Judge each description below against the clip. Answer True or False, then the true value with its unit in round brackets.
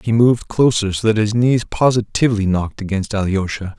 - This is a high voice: False (105 Hz)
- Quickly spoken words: False (175 wpm)